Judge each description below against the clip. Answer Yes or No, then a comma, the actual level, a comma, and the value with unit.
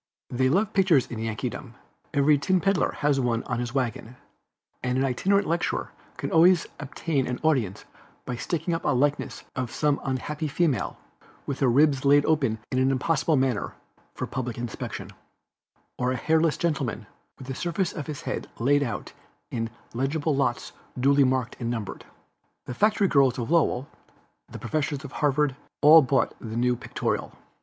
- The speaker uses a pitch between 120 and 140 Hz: Yes, low, 135 Hz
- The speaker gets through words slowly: No, average, 165 wpm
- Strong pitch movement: No, average, 3.7 semitones